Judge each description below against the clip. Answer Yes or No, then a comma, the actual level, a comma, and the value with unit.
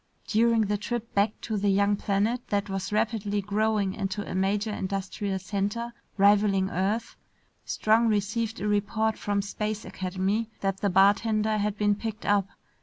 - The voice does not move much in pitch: Yes, narrow, 1.6 semitones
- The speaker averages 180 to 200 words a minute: No, average, 155 wpm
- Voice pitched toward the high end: Yes, high, 205 Hz